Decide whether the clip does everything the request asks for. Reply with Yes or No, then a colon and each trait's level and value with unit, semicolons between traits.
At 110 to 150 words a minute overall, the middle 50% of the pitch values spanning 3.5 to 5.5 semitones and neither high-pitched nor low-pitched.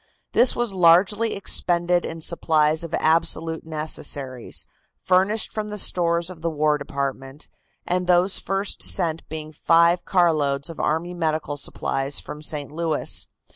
No: slow, 135 wpm; average, 2.8 semitones; medium, 165 Hz